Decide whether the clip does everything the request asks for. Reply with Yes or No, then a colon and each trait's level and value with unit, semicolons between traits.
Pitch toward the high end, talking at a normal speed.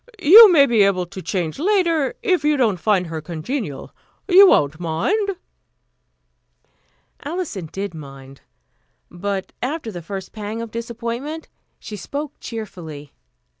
No: high, 215 Hz; slow, 130 wpm